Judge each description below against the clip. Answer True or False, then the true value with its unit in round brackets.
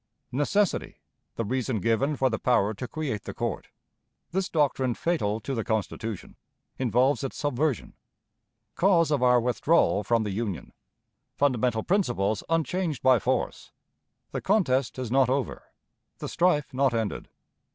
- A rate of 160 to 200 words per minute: False (140 wpm)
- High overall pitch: False (130 Hz)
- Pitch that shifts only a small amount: False (4.6 semitones)